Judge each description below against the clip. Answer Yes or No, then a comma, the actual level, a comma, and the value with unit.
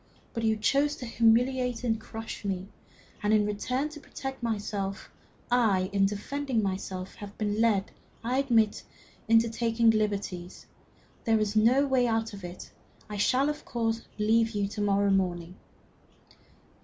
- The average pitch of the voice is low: No, high, 220 Hz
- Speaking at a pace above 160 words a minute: No, average, 155 wpm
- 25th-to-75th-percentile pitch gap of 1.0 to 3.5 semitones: Yes, average, 3.0 semitones